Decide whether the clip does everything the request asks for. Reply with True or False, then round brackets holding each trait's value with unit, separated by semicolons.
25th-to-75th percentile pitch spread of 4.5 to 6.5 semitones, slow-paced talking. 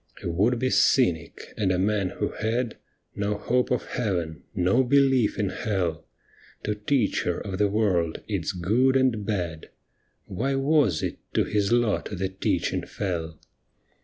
False (5.1 semitones; 155 wpm)